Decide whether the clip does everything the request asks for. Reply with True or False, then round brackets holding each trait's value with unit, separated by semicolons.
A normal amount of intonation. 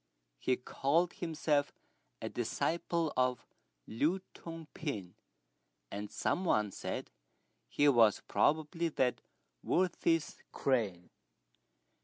False (5.7 semitones)